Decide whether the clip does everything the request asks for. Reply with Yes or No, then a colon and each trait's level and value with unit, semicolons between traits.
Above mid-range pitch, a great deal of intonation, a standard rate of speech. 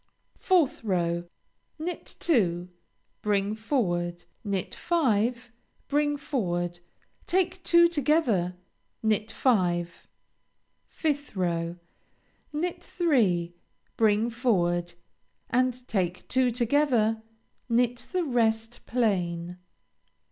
No: high, 225 Hz; wide, 7.8 semitones; slow, 85 wpm